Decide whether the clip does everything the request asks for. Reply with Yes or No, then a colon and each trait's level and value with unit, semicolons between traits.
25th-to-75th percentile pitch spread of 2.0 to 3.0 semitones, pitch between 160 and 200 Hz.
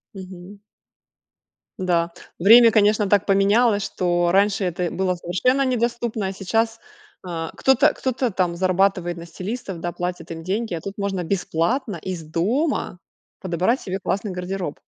No: average, 3.7 semitones; high, 190 Hz